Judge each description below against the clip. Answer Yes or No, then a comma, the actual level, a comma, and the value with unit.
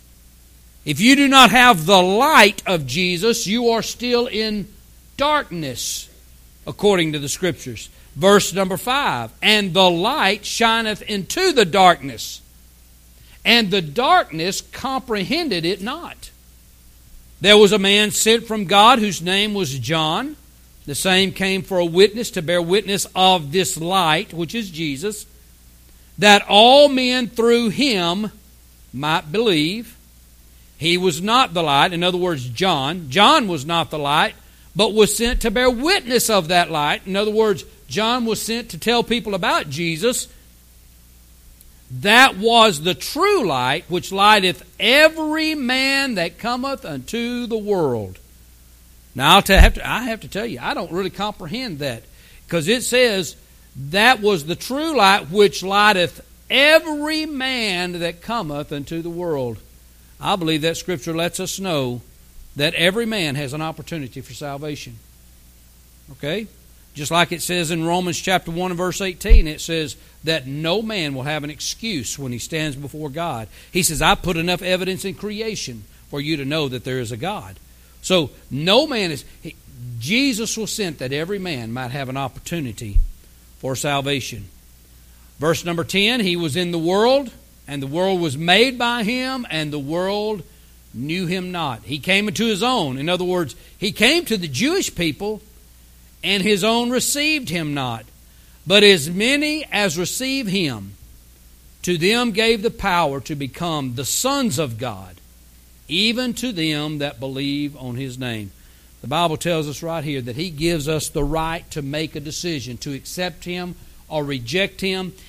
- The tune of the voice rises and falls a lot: Yes, wide, 7.8 semitones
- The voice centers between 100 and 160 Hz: No, medium, 175 Hz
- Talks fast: No, average, 160 wpm